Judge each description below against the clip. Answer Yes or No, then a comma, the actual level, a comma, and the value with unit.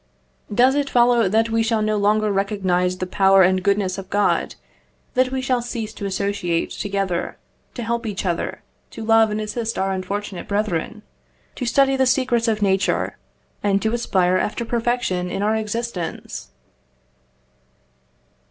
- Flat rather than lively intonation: No, average, 3.3 semitones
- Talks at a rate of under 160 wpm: Yes, average, 150 wpm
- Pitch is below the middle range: No, high, 210 Hz